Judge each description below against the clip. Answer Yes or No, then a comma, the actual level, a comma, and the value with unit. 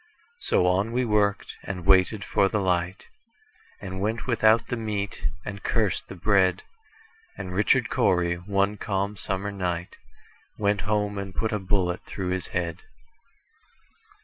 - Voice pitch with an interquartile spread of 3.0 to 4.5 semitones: No, narrow, 2.6 semitones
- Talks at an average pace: No, slow, 130 wpm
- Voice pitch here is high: No, low, 100 Hz